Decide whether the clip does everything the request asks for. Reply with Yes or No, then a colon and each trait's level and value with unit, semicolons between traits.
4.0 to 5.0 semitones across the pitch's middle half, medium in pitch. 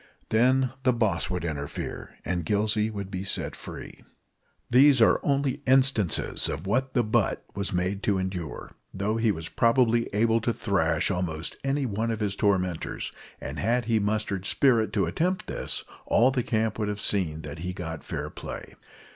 No: average, 4.3 semitones; low, 105 Hz